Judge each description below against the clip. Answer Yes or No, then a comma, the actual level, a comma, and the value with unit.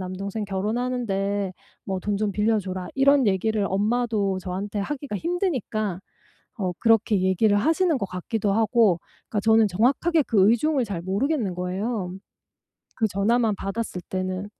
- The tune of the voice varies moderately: Yes, average, 3.6 semitones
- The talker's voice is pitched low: No, high, 210 Hz